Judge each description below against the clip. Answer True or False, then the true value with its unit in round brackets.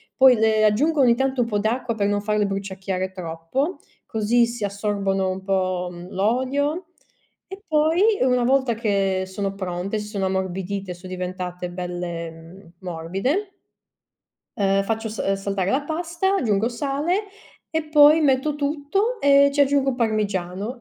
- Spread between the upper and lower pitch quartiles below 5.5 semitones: False (6.5 semitones)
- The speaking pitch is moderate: False (215 Hz)